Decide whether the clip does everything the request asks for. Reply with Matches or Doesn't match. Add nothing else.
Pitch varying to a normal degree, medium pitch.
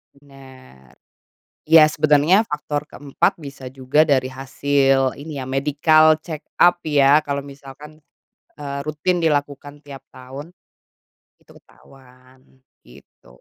Doesn't match